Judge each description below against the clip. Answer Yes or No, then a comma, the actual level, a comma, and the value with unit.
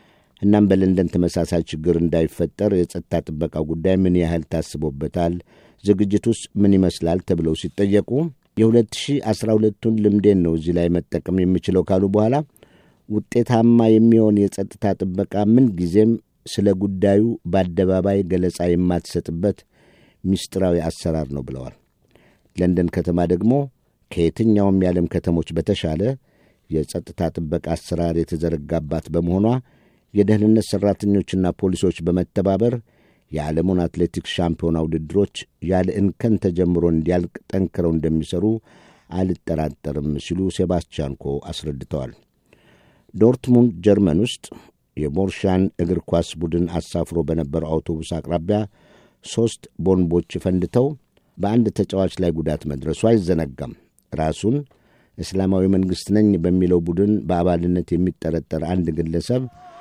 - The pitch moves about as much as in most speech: Yes, average, 3.5 semitones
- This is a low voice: Yes, very low, 90 Hz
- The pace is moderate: Yes, average, 100 wpm